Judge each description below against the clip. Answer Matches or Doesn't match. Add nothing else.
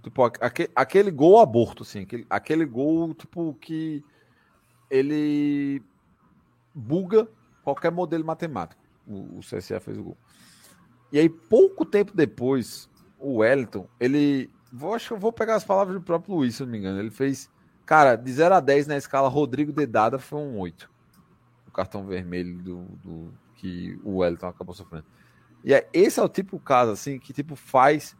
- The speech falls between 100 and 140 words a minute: Doesn't match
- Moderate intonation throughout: Doesn't match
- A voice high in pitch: Doesn't match